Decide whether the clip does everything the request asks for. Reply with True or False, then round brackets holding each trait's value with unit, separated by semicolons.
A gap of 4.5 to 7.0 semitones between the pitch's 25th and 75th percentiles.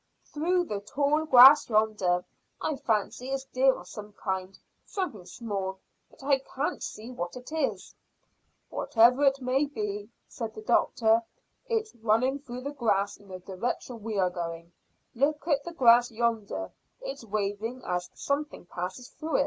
True (5.2 semitones)